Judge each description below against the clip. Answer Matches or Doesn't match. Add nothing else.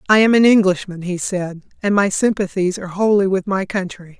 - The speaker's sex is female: Matches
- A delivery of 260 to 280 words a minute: Doesn't match